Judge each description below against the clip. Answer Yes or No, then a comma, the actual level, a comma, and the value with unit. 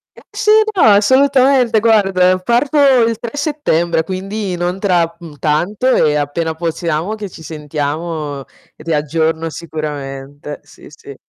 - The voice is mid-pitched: Yes, medium, 170 Hz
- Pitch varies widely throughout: Yes, wide, 5.7 semitones